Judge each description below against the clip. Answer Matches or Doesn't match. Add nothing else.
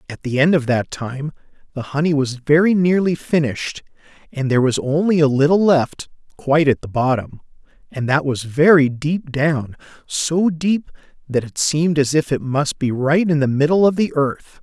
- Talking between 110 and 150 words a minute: Doesn't match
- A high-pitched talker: Doesn't match